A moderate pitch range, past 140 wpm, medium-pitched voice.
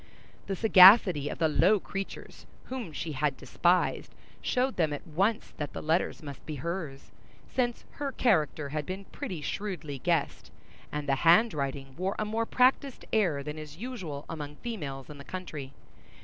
No: wide, 5.8 semitones; average, 165 wpm; medium, 165 Hz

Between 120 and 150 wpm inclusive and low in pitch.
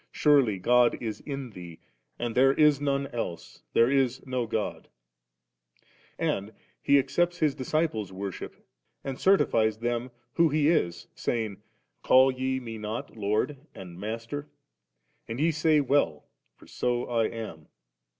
Yes: average, 140 wpm; low, 125 Hz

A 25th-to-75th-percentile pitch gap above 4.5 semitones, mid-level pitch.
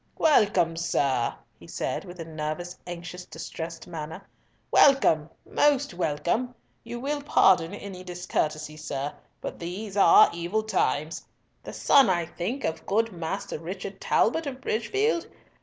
Yes: wide, 5.4 semitones; medium, 180 Hz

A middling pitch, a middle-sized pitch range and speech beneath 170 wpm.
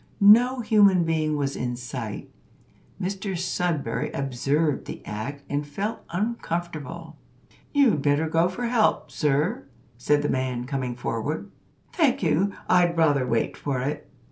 Yes: medium, 155 Hz; average, 4.9 semitones; slow, 135 wpm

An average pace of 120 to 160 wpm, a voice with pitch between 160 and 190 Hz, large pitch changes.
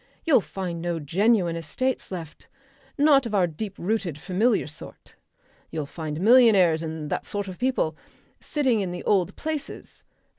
Yes: average, 150 wpm; medium, 185 Hz; wide, 5.8 semitones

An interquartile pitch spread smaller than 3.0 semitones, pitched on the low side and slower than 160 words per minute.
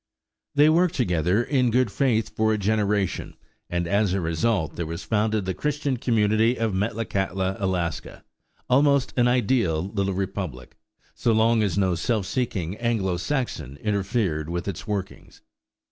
No: average, 4.1 semitones; low, 105 Hz; average, 145 wpm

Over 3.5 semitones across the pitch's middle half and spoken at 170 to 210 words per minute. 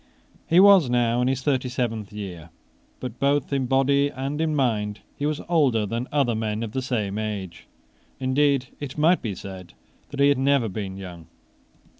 Yes: average, 4.8 semitones; average, 180 wpm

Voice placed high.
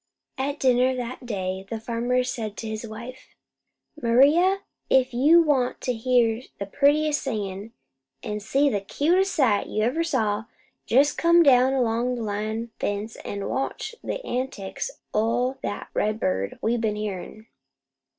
Yes: high, 240 Hz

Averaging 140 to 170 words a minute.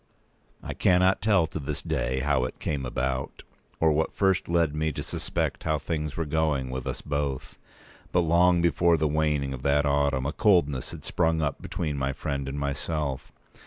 No: average, 185 wpm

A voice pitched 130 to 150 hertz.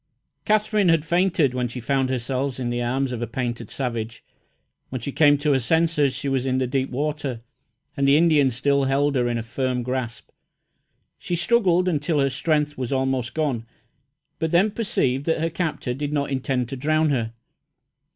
Yes: low, 135 Hz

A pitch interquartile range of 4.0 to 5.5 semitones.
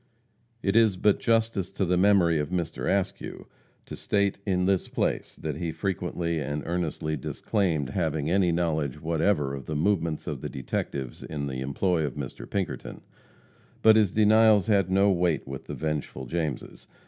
Yes: average, 4.5 semitones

